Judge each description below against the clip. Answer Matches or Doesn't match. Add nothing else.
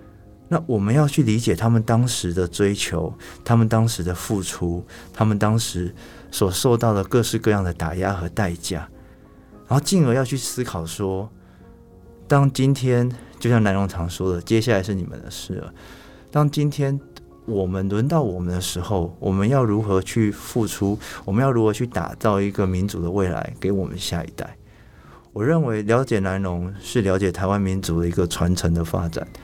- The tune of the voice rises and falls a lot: Doesn't match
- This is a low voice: Matches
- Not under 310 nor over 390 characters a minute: Doesn't match